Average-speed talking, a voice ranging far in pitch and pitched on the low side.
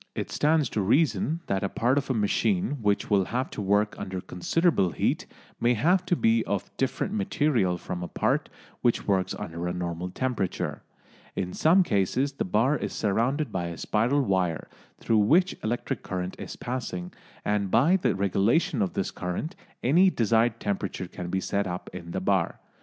Yes: average, 180 wpm; wide, 7.0 semitones; low, 105 Hz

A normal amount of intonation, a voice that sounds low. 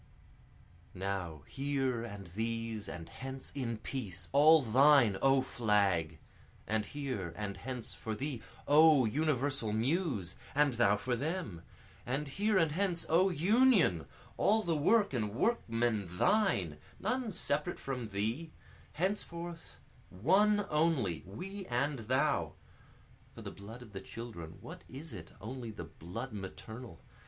No: wide, 7.1 semitones; low, 130 Hz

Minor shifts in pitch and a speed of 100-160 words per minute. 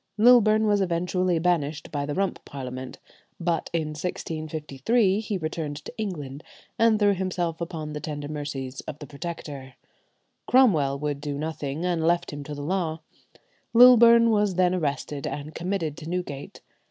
No: average, 4.4 semitones; average, 155 wpm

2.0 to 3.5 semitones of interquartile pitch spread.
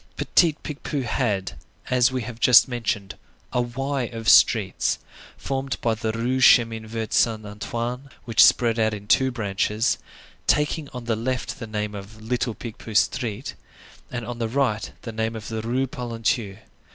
Yes: narrow, 2.5 semitones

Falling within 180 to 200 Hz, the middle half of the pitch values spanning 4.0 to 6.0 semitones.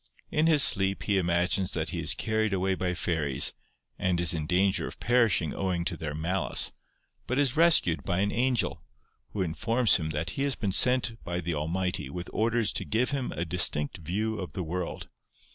No: very low, 95 Hz; average, 4.7 semitones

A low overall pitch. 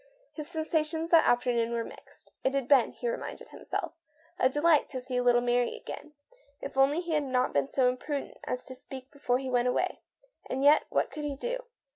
No: very high, 270 Hz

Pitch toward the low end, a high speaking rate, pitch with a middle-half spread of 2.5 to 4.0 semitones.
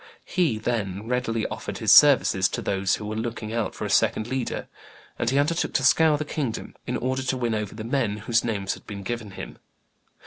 Yes: low, 115 Hz; fast, 210 wpm; average, 3.4 semitones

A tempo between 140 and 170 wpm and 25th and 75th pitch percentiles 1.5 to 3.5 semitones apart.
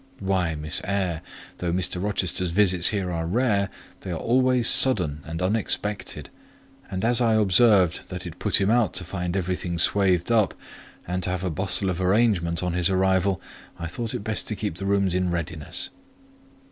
No: average, 180 wpm; average, 2.7 semitones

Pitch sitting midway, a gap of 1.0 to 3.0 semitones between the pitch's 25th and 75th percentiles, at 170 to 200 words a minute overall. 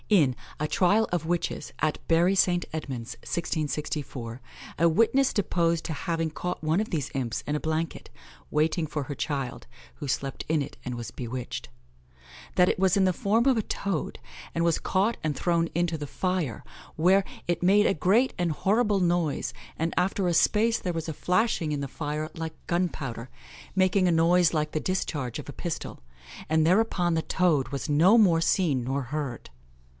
No: medium, 165 Hz; average, 3.6 semitones; average, 180 wpm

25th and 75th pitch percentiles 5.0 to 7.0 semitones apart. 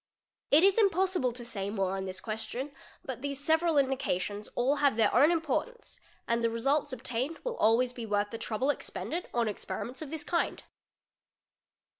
Yes: wide, 5.5 semitones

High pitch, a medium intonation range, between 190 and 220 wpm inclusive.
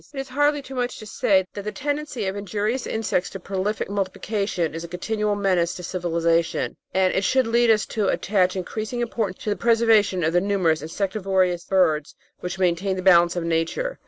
Yes: high, 195 Hz; average, 3.6 semitones; average, 195 wpm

